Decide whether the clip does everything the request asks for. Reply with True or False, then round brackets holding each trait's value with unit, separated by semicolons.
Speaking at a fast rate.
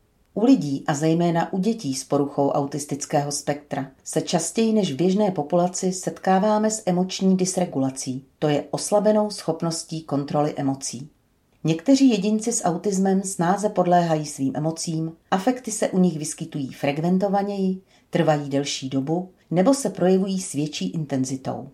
False (135 wpm)